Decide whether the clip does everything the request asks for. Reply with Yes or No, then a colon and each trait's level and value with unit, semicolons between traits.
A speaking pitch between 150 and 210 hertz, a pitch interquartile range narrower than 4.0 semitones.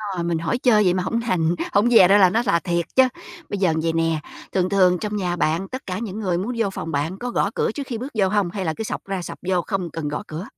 Yes: medium, 185 Hz; average, 3.6 semitones